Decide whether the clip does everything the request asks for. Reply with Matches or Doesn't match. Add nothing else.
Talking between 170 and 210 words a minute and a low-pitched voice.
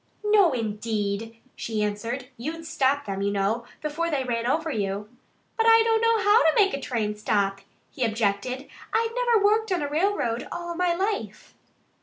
Doesn't match